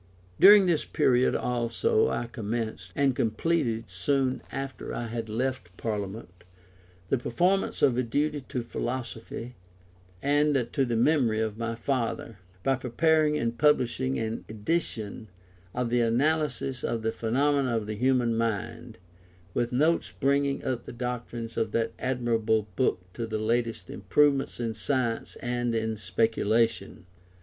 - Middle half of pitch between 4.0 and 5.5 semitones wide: No, average, 3.2 semitones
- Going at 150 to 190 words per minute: No, average, 140 wpm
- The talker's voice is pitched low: Yes, low, 120 Hz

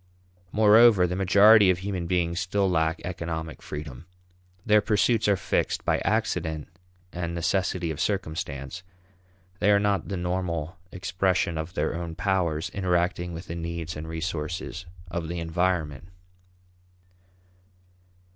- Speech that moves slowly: Yes, slow, 125 wpm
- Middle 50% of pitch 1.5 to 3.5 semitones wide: Yes, narrow, 2.6 semitones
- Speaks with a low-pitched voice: Yes, very low, 90 Hz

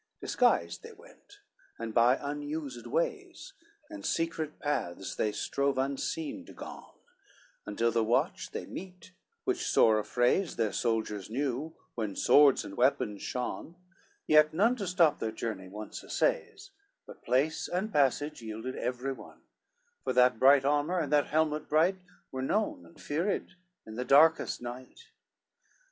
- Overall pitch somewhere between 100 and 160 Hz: Yes, medium, 140 Hz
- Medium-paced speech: Yes, average, 145 wpm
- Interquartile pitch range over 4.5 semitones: Yes, average, 5.3 semitones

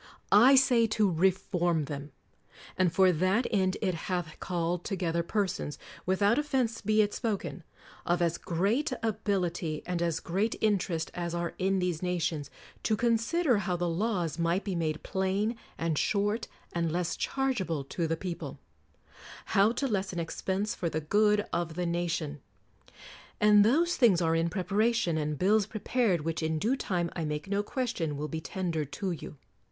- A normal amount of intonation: Yes, average, 4.0 semitones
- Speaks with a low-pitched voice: No, medium, 185 Hz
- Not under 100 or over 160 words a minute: No, average, 170 wpm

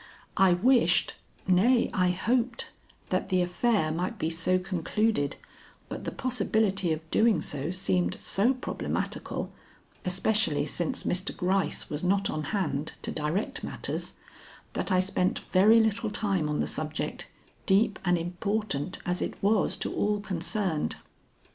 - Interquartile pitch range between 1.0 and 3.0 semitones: No, average, 4.1 semitones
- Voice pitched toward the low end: No, medium, 185 Hz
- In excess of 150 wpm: No, average, 140 wpm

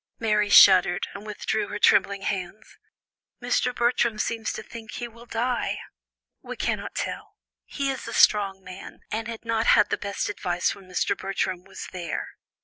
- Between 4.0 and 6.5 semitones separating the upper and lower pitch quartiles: No, average, 3.1 semitones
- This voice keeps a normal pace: Yes, average, 165 wpm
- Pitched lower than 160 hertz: No, high, 210 Hz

